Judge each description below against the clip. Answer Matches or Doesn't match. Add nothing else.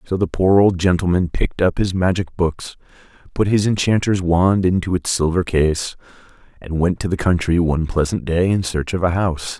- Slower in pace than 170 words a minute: Doesn't match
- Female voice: Doesn't match